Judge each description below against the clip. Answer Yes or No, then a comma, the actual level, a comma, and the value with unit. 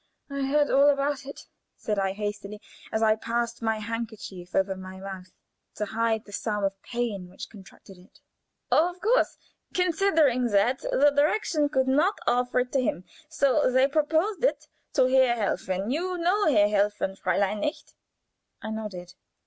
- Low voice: No, high, 235 Hz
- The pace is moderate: Yes, average, 170 wpm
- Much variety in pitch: Yes, wide, 6.0 semitones